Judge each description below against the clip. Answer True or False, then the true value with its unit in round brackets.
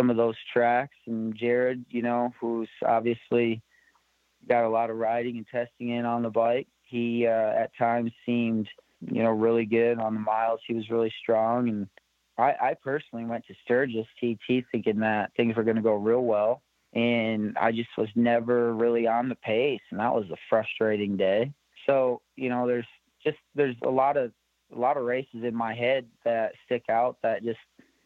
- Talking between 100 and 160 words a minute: False (190 wpm)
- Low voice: True (115 Hz)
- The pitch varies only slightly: True (1.2 semitones)